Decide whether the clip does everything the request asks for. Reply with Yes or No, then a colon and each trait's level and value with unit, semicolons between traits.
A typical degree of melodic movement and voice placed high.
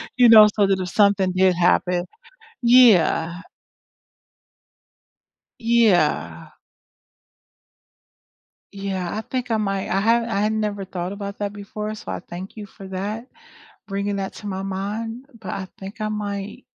No: narrow, 2.2 semitones; high, 200 Hz